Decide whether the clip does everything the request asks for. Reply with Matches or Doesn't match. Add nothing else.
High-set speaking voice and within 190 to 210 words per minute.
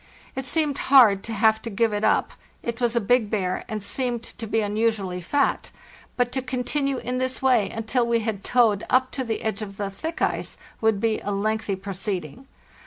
Matches